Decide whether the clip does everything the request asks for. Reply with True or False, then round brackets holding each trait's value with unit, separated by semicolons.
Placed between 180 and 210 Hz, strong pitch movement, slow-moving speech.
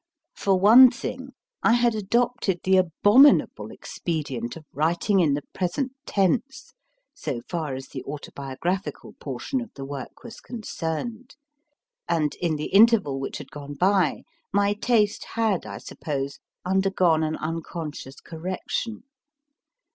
True (185 Hz; 6.5 semitones; 130 wpm)